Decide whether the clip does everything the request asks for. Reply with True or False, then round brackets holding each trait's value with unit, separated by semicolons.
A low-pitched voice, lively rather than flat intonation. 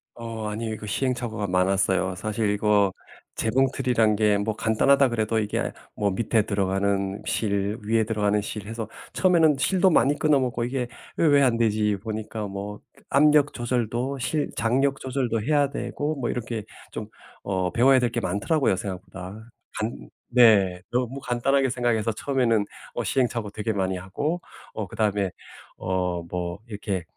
False (110 Hz; 3.9 semitones)